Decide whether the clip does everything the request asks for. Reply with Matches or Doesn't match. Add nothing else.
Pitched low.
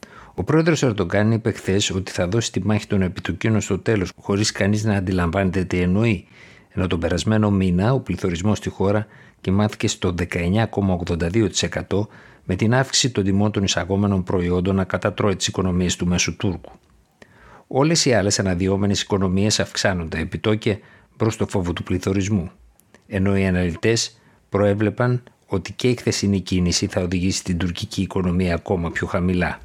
Matches